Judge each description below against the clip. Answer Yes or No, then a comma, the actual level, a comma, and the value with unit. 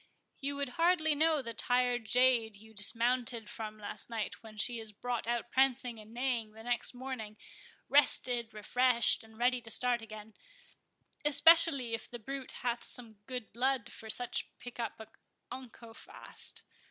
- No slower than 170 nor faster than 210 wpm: No, average, 155 wpm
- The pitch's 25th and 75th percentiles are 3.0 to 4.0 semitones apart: No, narrow, 2.6 semitones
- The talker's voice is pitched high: Yes, high, 240 Hz